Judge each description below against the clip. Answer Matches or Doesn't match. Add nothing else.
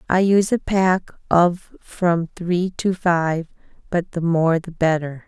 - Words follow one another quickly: Doesn't match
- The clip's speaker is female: Matches